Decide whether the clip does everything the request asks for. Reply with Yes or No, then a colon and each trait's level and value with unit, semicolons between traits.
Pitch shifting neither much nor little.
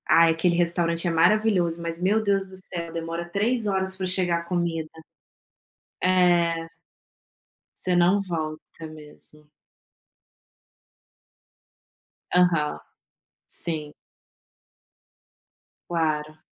No: narrow, 2.1 semitones